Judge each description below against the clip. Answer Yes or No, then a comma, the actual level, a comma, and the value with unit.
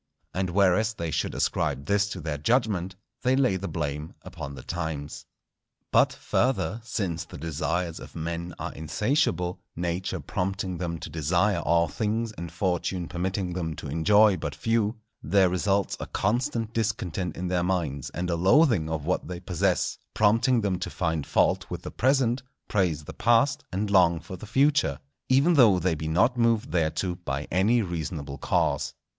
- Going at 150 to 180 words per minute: Yes, average, 170 wpm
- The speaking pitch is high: No, very low, 90 Hz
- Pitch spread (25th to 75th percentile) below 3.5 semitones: No, average, 4.6 semitones